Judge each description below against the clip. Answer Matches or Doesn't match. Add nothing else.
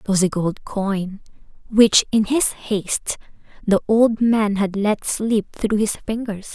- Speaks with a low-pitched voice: Doesn't match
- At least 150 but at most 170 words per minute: Matches